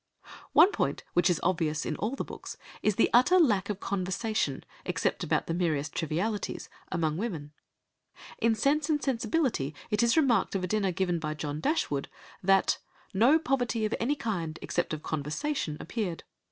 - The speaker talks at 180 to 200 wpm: No, average, 165 wpm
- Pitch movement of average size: No, wide, 6.6 semitones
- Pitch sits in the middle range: No, high, 195 Hz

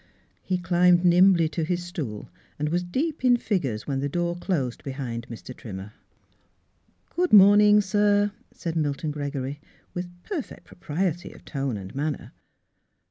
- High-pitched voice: No, medium, 170 Hz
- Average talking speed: Yes, average, 150 wpm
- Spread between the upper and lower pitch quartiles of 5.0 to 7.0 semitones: Yes, wide, 5.4 semitones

